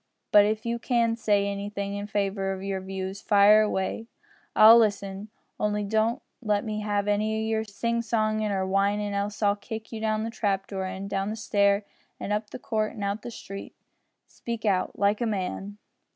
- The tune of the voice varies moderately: No, narrow, 1.6 semitones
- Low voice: No, high, 210 Hz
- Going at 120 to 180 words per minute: No, average, 195 wpm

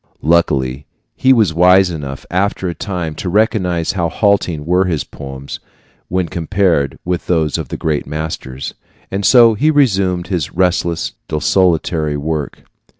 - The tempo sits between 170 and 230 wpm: No, average, 145 wpm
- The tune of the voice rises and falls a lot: No, average, 3.7 semitones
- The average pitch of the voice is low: Yes, very low, 85 Hz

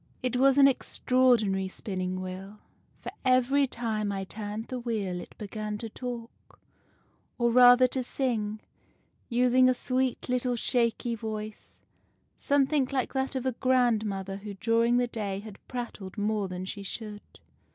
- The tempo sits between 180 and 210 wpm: No, average, 145 wpm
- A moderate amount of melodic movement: Yes, average, 3.5 semitones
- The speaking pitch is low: No, high, 230 Hz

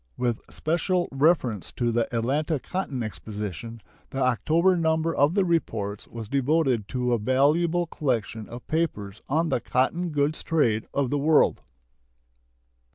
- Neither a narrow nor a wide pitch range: No, wide, 5.7 semitones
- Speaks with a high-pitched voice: No, low, 135 Hz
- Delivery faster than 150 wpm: No, average, 140 wpm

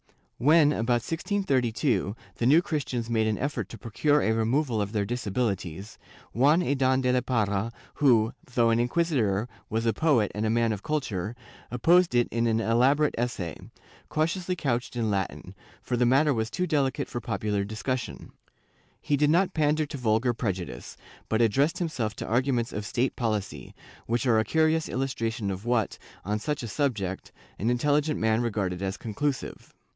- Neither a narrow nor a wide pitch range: Yes, average, 4.7 semitones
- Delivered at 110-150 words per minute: No, average, 170 wpm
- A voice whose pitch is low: Yes, low, 120 Hz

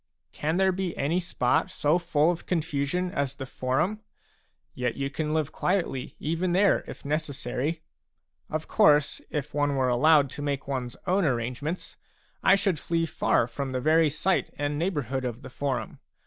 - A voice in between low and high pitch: Yes, medium, 150 Hz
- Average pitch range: Yes, average, 3.8 semitones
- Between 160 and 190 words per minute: Yes, average, 170 wpm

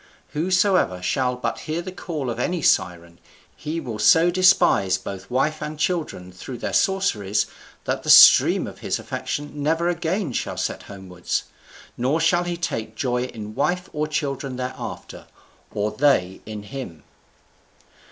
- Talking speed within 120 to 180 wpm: Yes, average, 150 wpm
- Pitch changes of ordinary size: No, wide, 7.7 semitones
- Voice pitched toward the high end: No, low, 135 Hz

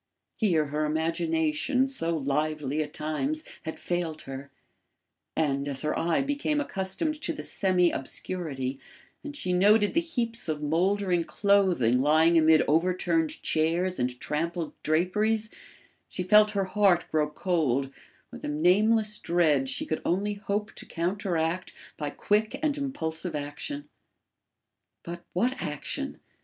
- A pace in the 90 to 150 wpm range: Yes, slow, 135 wpm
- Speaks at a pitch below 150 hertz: No, medium, 175 Hz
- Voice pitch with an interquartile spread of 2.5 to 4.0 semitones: No, average, 5.1 semitones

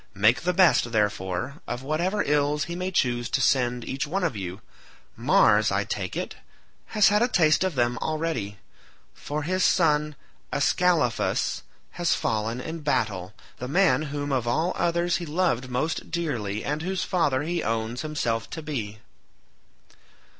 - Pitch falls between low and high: Yes, medium, 145 Hz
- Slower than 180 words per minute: Yes, average, 155 wpm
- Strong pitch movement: Yes, wide, 6.6 semitones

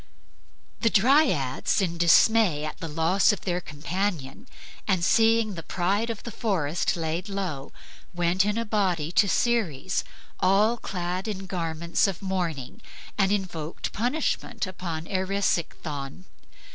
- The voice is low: No, medium, 185 Hz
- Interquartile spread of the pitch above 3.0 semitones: Yes, average, 3.9 semitones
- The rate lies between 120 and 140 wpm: Yes, slow, 135 wpm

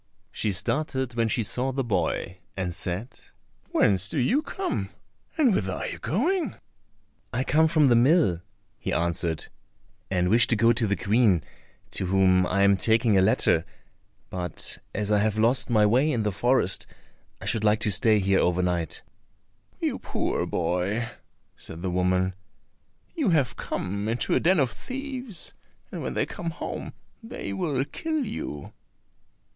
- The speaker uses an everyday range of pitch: No, wide, 6.6 semitones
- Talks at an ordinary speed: Yes, average, 160 wpm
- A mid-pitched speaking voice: No, low, 110 Hz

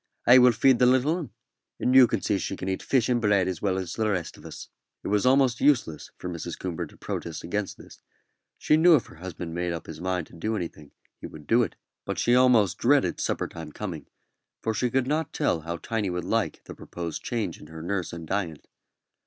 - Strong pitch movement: Yes, wide, 6.5 semitones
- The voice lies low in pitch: Yes, low, 100 Hz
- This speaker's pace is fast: Yes, fast, 225 wpm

